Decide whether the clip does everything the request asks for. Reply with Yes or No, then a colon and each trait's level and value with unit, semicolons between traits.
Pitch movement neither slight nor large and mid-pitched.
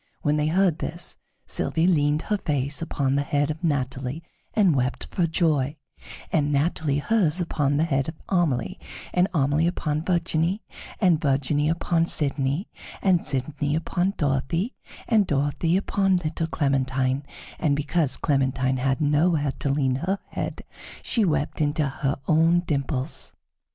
Yes: average, 3.4 semitones; medium, 150 Hz